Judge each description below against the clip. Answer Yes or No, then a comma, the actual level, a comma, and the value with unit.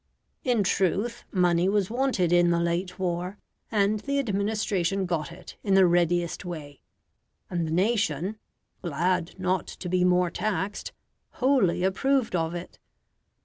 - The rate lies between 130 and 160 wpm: Yes, average, 140 wpm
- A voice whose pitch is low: No, medium, 185 Hz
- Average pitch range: Yes, average, 3.1 semitones